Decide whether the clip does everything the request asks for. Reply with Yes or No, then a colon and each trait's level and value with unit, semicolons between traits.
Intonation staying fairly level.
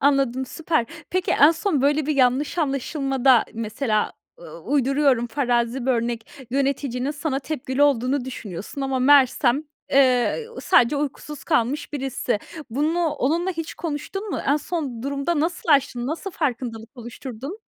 No: average, 3.3 semitones